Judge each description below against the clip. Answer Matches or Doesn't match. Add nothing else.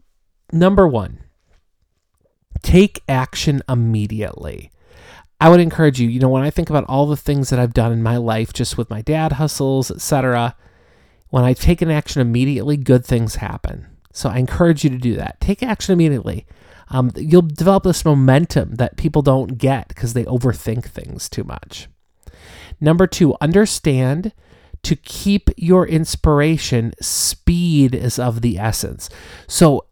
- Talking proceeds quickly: Doesn't match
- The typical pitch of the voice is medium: Doesn't match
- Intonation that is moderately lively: Doesn't match